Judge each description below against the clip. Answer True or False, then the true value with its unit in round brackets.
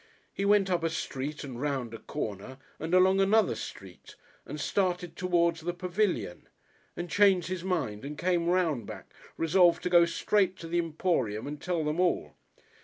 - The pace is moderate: True (175 wpm)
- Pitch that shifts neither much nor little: True (4.0 semitones)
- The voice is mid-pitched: True (170 Hz)